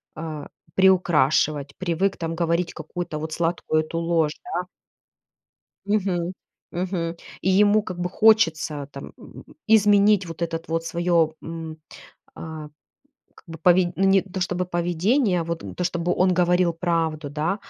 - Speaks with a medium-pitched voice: Yes, medium, 170 Hz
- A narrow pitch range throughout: Yes, narrow, 2.3 semitones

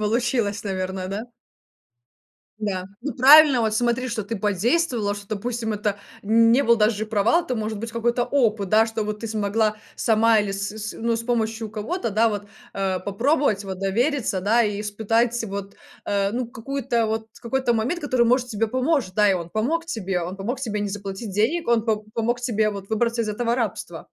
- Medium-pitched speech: No, high, 220 Hz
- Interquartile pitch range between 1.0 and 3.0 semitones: Yes, average, 2.7 semitones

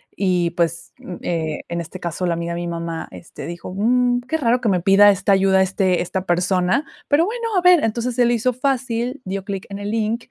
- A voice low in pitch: No, high, 195 Hz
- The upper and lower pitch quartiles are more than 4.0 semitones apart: Yes, wide, 5.5 semitones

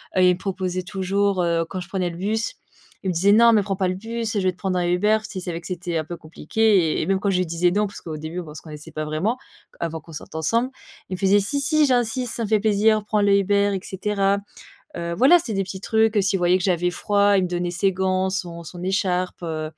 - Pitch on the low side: No, high, 190 Hz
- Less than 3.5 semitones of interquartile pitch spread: Yes, average, 2.8 semitones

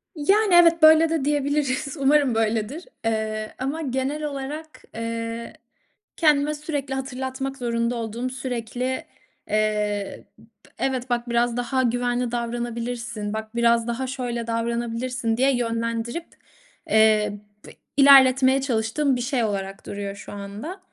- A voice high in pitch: Yes, high, 245 Hz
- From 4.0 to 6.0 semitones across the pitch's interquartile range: No, average, 3.1 semitones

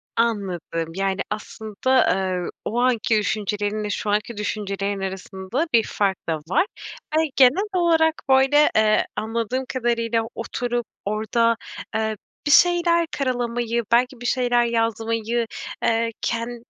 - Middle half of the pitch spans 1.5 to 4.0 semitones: Yes, average, 3.1 semitones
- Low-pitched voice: No, high, 230 Hz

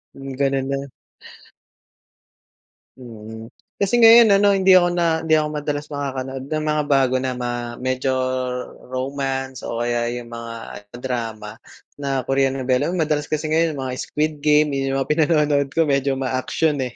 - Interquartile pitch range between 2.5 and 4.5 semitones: Yes, average, 2.9 semitones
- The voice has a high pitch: No, low, 135 Hz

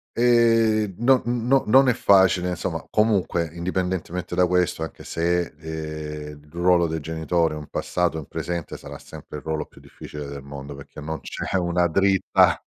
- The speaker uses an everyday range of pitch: Yes, average, 3.7 semitones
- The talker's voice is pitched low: Yes, very low, 85 Hz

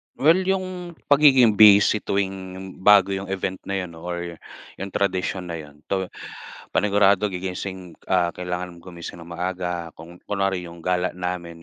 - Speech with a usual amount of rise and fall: No, narrow, 2.2 semitones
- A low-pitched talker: Yes, very low, 95 Hz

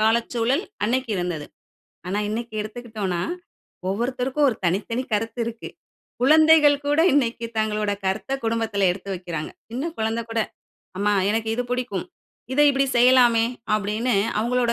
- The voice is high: Yes, high, 230 Hz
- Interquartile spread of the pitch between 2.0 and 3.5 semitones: Yes, average, 3.1 semitones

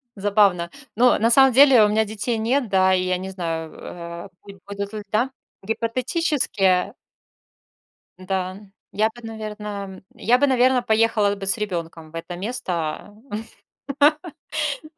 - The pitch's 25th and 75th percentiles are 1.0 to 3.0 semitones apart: No, average, 3.7 semitones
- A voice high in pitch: Yes, high, 205 Hz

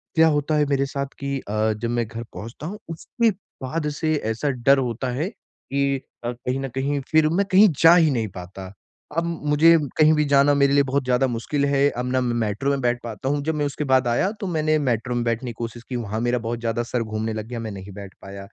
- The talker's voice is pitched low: Yes, low, 130 Hz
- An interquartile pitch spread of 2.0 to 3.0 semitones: No, average, 4.0 semitones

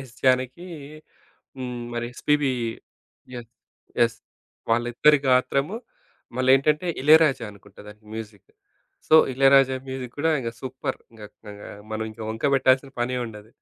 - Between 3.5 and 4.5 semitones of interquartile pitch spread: No, average, 3.1 semitones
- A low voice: Yes, low, 130 Hz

